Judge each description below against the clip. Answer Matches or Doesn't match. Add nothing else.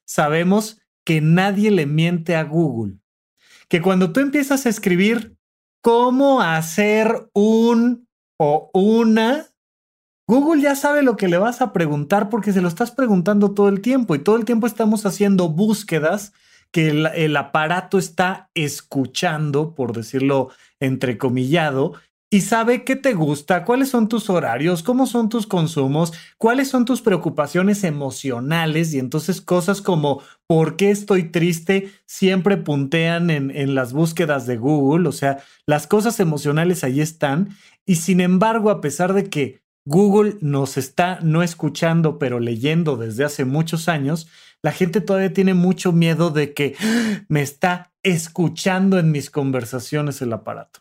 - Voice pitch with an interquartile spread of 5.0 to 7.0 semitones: Matches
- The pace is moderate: Matches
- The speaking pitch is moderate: Matches